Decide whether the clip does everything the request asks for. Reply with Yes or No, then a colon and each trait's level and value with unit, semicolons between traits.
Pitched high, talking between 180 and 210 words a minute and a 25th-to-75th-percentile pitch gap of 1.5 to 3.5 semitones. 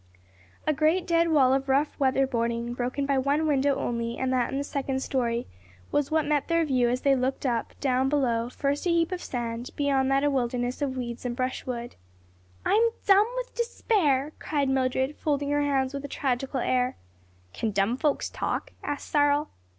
Yes: very high, 270 Hz; average, 190 wpm; narrow, 2.6 semitones